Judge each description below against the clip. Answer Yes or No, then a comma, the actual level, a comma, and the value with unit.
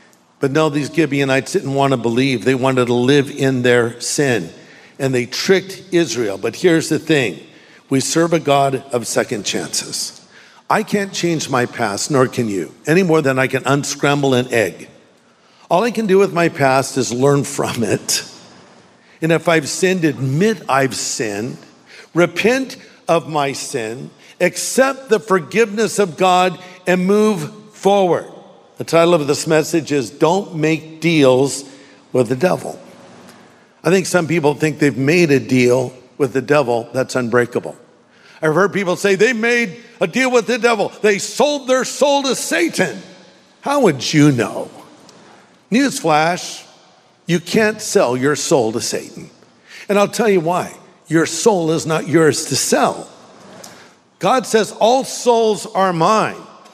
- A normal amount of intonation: No, wide, 6.4 semitones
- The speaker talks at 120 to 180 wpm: Yes, average, 160 wpm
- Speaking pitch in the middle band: Yes, medium, 160 Hz